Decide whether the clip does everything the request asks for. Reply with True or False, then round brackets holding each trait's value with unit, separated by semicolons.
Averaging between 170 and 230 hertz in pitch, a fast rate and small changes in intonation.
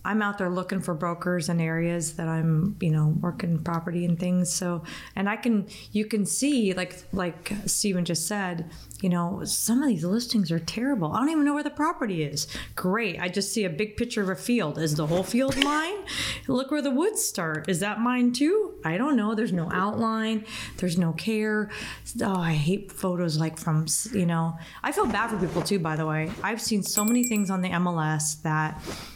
False (190 Hz; 210 wpm; 4.6 semitones)